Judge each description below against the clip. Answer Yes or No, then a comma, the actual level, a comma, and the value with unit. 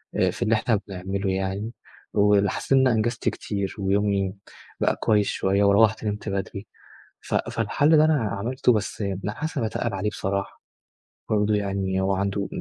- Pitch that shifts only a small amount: Yes, narrow, 1.9 semitones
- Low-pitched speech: Yes, low, 100 Hz